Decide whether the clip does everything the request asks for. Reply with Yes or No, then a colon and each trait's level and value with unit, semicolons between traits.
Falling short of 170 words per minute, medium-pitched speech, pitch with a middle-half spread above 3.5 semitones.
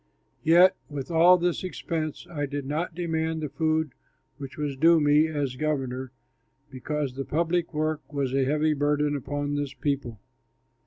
No: average, 155 wpm; medium, 150 Hz; narrow, 2.4 semitones